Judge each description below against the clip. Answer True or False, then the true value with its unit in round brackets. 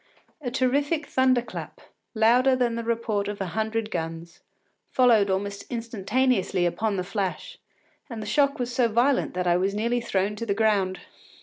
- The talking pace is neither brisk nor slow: True (170 wpm)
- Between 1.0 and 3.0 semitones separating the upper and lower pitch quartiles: False (3.8 semitones)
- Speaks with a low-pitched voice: False (220 Hz)